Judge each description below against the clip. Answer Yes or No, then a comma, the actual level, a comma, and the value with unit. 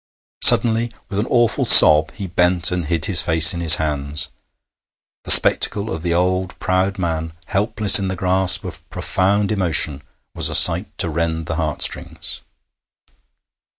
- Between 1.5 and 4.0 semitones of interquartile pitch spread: Yes, average, 3.1 semitones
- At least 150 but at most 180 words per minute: Yes, average, 155 wpm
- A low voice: Yes, very low, 90 Hz